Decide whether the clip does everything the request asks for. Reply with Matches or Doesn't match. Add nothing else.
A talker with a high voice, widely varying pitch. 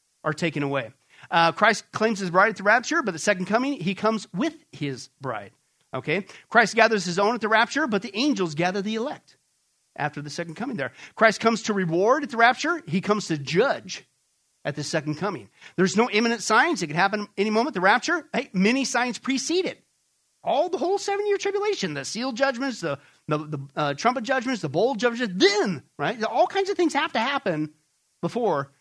Matches